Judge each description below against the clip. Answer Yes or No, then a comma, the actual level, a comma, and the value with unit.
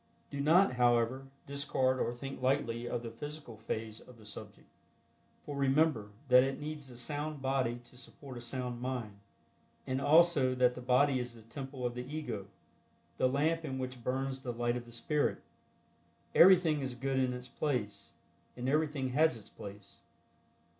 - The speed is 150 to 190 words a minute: Yes, average, 170 wpm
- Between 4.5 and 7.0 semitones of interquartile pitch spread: No, average, 2.8 semitones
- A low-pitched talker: Yes, low, 130 Hz